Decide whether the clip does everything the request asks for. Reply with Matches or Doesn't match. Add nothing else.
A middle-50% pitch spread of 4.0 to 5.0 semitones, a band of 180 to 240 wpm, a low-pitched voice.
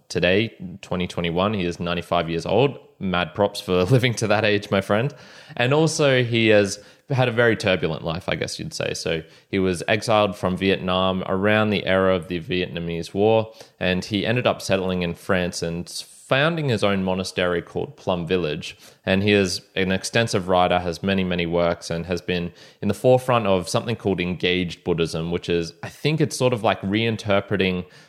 Doesn't match